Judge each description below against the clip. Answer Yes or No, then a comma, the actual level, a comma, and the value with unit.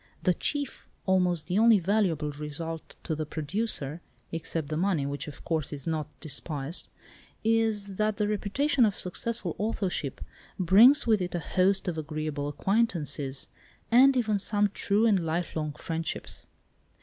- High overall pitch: No, medium, 180 Hz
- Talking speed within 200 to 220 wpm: No, average, 145 wpm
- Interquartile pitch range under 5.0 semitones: No, wide, 5.5 semitones